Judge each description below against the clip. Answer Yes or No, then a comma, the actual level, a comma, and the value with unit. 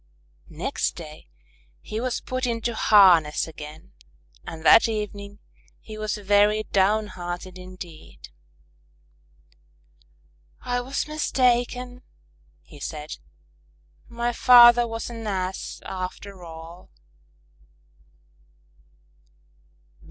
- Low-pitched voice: No, high, 205 Hz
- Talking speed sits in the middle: No, slow, 85 wpm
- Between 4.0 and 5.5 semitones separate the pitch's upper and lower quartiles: Yes, average, 5.1 semitones